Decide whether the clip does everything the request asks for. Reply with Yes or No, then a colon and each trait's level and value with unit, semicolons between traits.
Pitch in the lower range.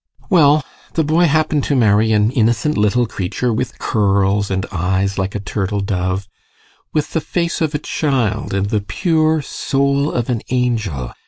Yes: low, 115 Hz